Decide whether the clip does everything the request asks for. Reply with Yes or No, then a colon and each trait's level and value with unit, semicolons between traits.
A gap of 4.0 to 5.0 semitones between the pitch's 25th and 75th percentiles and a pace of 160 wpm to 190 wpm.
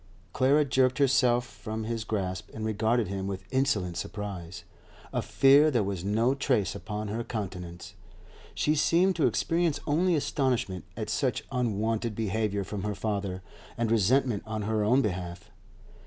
No: average, 4.7 semitones; average, 150 wpm